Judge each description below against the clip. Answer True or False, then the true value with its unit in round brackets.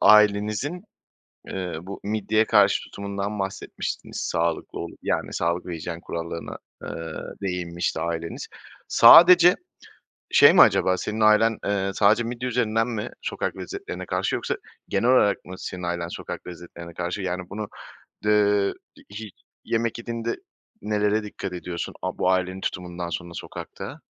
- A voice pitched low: True (100 Hz)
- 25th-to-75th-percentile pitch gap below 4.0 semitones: True (3.4 semitones)